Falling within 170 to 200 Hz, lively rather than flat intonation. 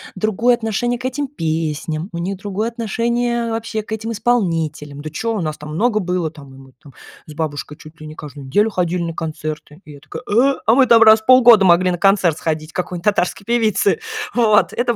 Yes: high, 190 Hz; wide, 6.6 semitones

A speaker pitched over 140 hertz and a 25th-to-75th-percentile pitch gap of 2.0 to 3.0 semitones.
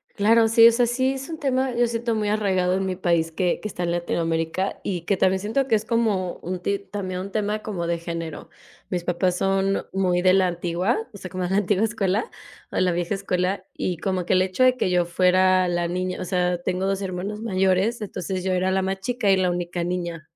Yes: medium, 185 Hz; narrow, 2.6 semitones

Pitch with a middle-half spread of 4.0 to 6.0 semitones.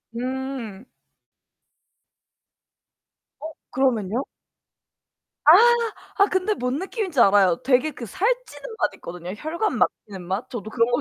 No: wide, 7.5 semitones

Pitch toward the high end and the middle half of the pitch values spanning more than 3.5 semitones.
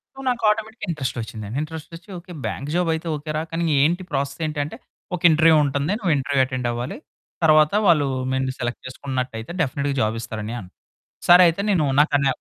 No: medium, 145 Hz; average, 4.3 semitones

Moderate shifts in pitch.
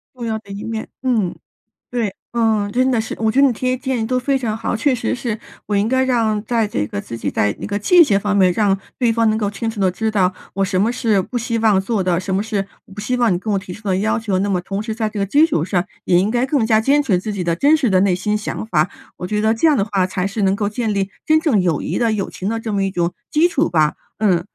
Yes: average, 3.3 semitones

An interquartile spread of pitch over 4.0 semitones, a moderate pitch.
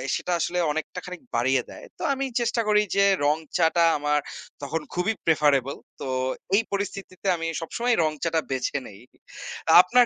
Yes: average, 5.1 semitones; medium, 165 Hz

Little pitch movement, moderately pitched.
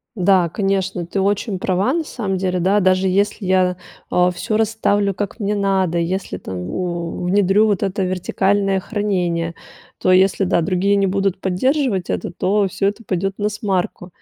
No: narrow, 2.0 semitones; high, 195 Hz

